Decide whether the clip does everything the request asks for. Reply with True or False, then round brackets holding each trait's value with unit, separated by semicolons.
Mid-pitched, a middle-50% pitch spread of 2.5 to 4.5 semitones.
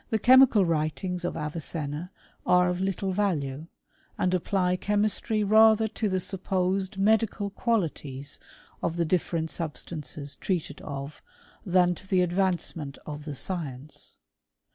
True (180 Hz; 4.2 semitones)